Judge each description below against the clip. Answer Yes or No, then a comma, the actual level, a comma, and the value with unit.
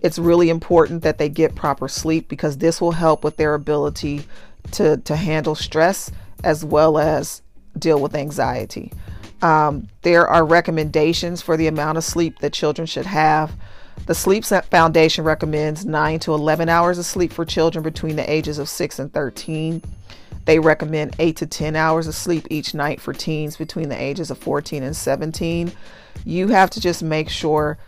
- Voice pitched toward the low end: No, medium, 155 Hz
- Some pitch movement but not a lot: No, narrow, 1.8 semitones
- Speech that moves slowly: No, average, 175 wpm